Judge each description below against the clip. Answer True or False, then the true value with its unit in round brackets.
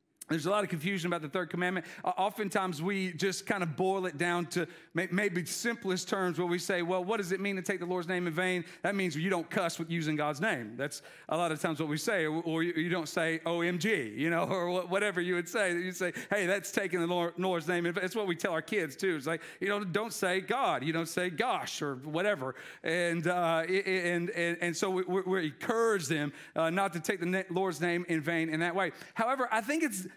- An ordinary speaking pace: False (240 wpm)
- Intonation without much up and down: True (2.3 semitones)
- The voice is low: False (180 Hz)